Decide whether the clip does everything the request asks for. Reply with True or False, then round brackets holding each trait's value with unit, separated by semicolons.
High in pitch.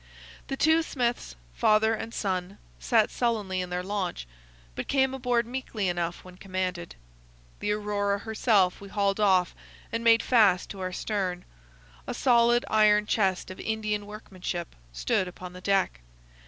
True (205 Hz)